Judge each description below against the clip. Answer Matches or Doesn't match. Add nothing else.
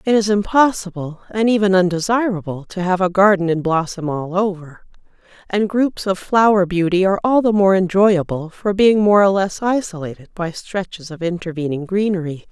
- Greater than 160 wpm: Matches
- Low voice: Doesn't match